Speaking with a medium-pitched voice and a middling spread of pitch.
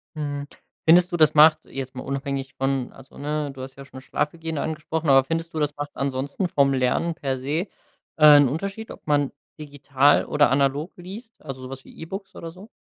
Yes: medium, 145 Hz; average, 3.0 semitones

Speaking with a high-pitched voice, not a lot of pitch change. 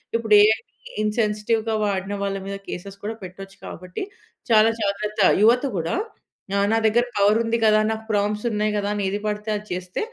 Yes: high, 210 Hz; narrow, 1.8 semitones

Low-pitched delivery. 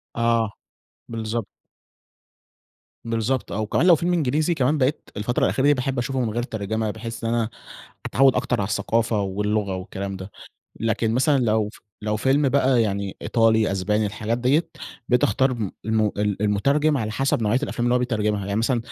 Yes: low, 115 Hz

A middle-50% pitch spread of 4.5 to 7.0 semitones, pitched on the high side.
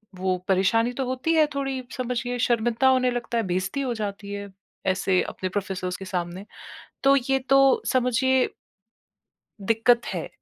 Yes: average, 5.1 semitones; high, 235 Hz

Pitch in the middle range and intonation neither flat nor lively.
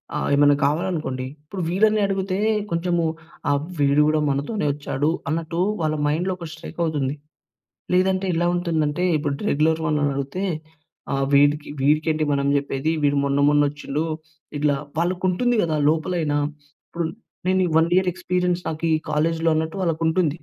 Yes: medium, 160 Hz; average, 3.3 semitones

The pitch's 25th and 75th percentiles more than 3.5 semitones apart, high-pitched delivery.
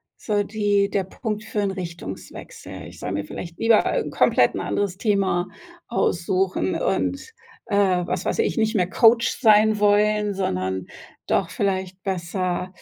No: average, 2.7 semitones; high, 200 Hz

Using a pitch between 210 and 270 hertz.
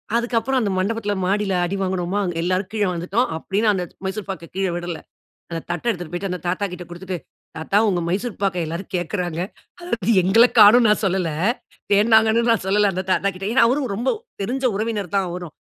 No: high, 195 Hz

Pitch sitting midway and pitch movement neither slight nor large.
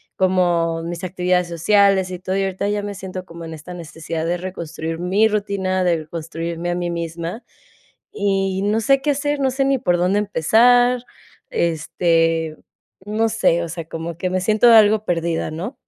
Yes: medium, 180 Hz; average, 3.6 semitones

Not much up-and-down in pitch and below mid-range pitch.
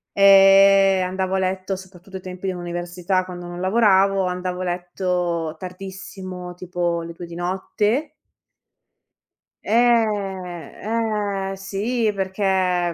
No: narrow, 1.7 semitones; high, 190 Hz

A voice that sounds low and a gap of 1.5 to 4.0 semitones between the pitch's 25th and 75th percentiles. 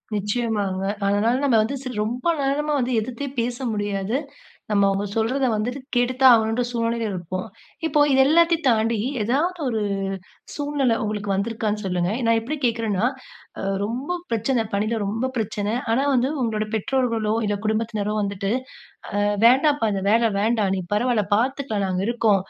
No: high, 225 Hz; average, 3.4 semitones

